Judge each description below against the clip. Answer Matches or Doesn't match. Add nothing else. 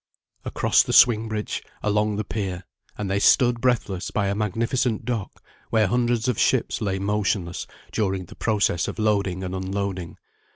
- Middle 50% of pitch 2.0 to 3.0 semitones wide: Matches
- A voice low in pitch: Matches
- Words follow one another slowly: Doesn't match